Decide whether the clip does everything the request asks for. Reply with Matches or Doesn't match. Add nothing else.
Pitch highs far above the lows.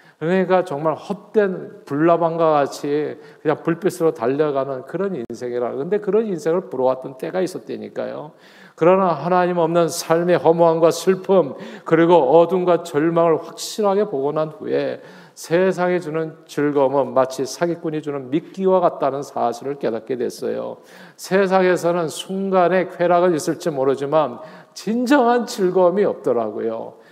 Doesn't match